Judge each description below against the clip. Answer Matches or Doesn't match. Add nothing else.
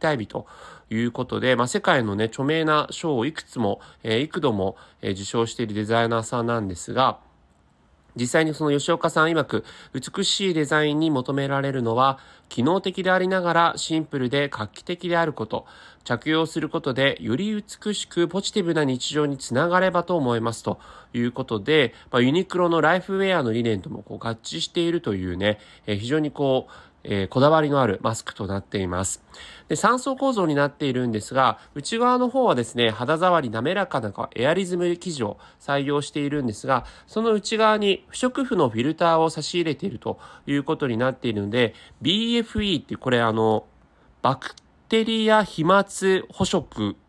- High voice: Doesn't match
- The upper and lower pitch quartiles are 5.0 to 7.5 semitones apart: Matches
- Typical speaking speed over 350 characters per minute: Matches